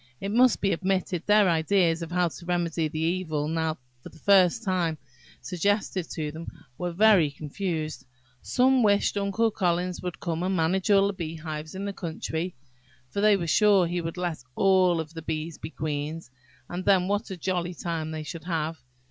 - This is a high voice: No, medium, 175 Hz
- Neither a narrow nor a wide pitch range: Yes, average, 3.2 semitones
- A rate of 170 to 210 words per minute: Yes, average, 180 wpm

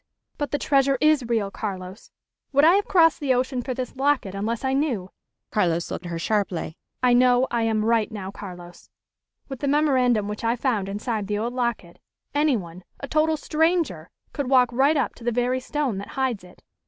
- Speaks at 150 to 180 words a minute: No, average, 195 wpm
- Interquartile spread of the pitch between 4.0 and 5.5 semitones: Yes, average, 5.2 semitones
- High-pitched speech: Yes, high, 245 Hz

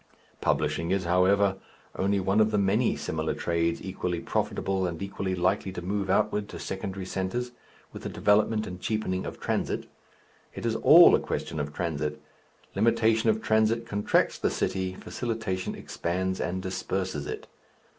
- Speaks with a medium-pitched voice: No, very low, 95 Hz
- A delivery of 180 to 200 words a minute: No, average, 155 wpm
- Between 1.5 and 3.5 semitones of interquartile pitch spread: Yes, narrow, 2.6 semitones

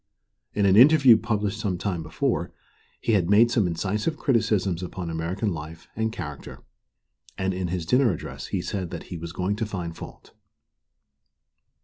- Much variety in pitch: No, average, 4.4 semitones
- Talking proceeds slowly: No, average, 160 wpm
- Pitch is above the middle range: No, very low, 95 Hz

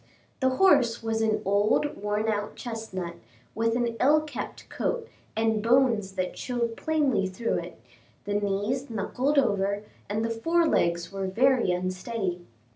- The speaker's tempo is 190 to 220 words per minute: No, average, 145 wpm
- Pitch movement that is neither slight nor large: Yes, average, 4.3 semitones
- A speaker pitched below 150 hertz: No, high, 225 Hz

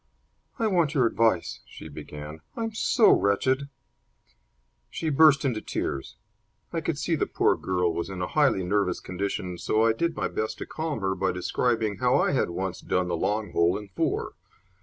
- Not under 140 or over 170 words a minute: No, average, 180 wpm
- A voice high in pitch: No, low, 105 Hz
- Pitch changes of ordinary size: No, wide, 7.6 semitones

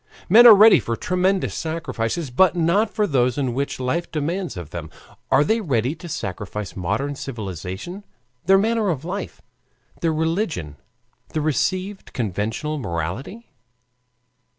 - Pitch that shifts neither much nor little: No, wide, 8.5 semitones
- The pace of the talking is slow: Yes, slow, 130 wpm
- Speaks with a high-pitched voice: No, medium, 150 Hz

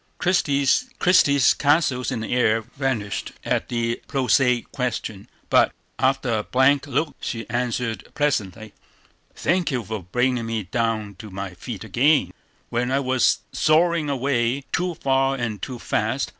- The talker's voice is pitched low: Yes, low, 125 Hz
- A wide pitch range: No, average, 3.7 semitones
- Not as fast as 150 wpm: Yes, average, 140 wpm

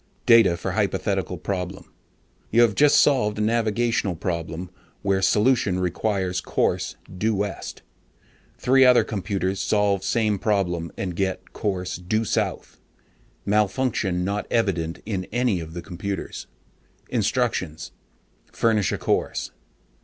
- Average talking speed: No, slow, 120 wpm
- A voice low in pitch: Yes, low, 100 Hz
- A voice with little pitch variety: No, average, 3.4 semitones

